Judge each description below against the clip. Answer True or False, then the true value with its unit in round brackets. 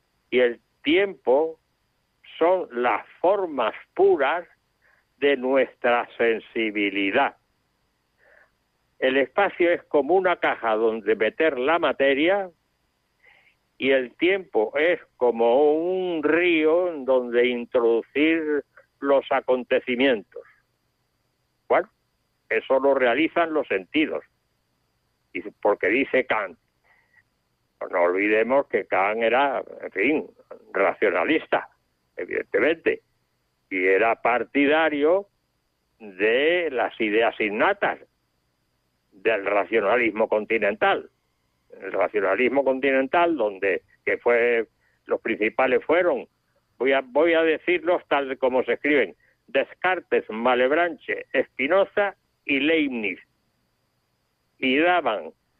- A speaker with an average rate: False (90 wpm)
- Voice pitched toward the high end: False (155 Hz)